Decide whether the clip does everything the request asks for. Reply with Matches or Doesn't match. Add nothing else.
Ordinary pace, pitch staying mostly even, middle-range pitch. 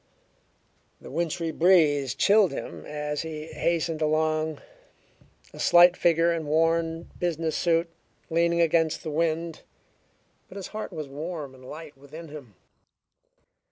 Doesn't match